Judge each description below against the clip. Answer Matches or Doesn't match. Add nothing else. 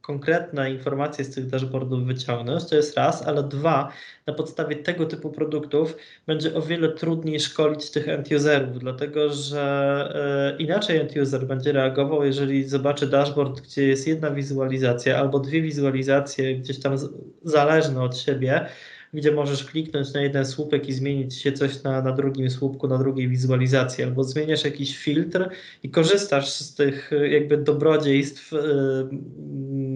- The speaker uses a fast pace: Doesn't match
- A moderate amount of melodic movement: Doesn't match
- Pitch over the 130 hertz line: Matches